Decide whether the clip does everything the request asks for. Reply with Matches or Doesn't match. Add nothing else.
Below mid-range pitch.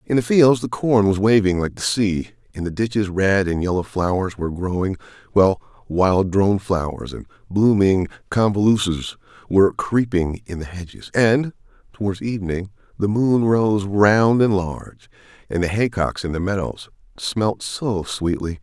Matches